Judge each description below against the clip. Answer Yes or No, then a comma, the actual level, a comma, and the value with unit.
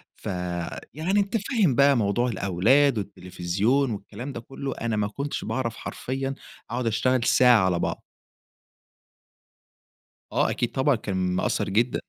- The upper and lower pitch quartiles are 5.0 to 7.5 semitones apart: Yes, wide, 5.4 semitones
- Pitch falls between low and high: No, low, 120 Hz